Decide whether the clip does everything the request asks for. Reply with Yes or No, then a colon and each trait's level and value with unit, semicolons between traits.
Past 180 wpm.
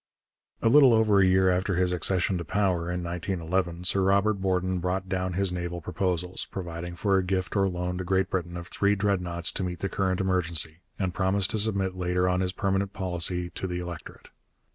Yes: average, 200 wpm